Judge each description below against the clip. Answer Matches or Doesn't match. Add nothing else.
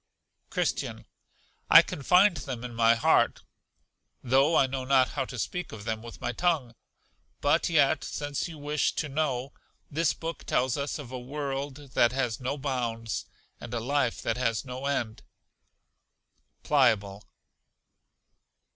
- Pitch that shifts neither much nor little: Matches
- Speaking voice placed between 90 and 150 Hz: Matches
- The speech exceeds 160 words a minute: Doesn't match